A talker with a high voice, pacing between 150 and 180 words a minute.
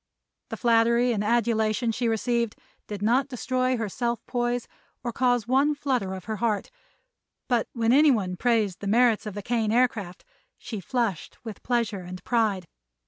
Yes: high, 230 Hz; average, 160 wpm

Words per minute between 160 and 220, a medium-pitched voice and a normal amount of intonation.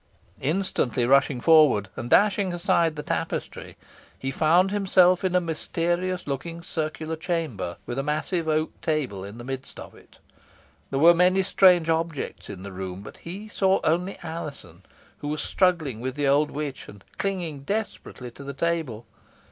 Yes: average, 165 wpm; medium, 155 Hz; average, 4.8 semitones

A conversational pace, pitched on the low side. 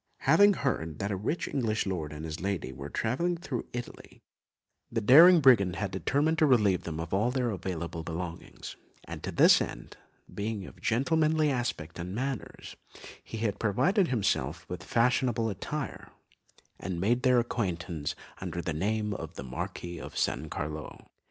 Yes: average, 160 wpm; low, 105 Hz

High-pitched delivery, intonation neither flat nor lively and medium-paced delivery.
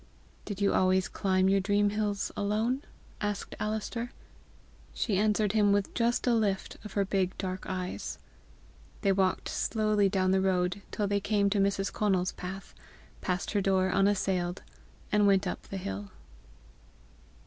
No: high, 200 Hz; narrow, 1.7 semitones; average, 150 wpm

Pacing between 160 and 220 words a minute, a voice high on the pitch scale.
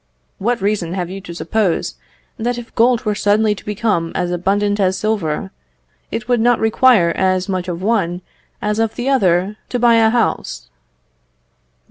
Yes: average, 165 wpm; high, 210 Hz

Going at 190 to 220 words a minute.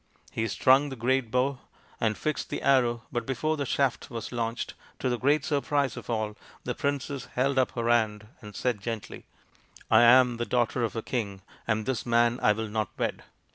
Yes: average, 200 wpm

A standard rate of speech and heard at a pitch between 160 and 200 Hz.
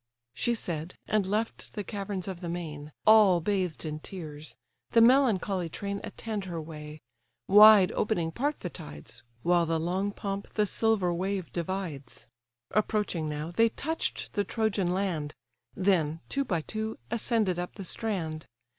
Yes: average, 150 wpm; medium, 185 Hz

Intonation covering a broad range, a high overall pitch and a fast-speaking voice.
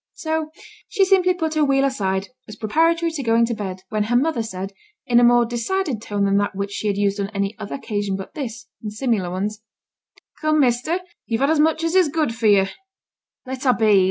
Yes: wide, 7.1 semitones; high, 235 Hz; fast, 215 wpm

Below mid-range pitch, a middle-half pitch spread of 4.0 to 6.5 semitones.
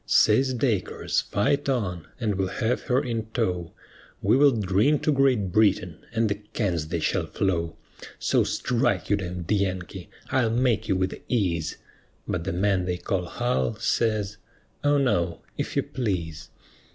Yes: low, 105 Hz; average, 4.9 semitones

